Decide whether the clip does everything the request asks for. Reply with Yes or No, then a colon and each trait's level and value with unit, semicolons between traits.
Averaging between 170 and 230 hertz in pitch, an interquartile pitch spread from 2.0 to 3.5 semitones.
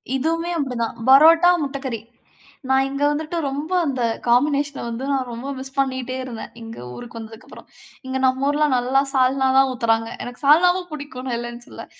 No: very high, 265 Hz; average, 2.9 semitones